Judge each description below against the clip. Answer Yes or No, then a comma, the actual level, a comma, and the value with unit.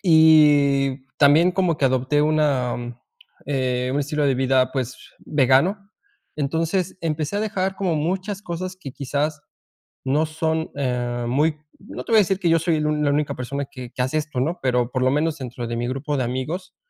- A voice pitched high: No, medium, 150 Hz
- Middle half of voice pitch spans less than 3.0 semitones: No, average, 3.9 semitones